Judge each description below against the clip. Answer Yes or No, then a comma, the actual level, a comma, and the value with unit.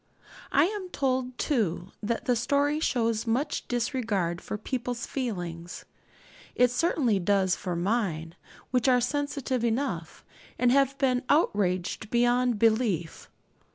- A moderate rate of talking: No, slow, 120 wpm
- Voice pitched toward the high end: Yes, high, 240 Hz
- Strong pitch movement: No, average, 4.7 semitones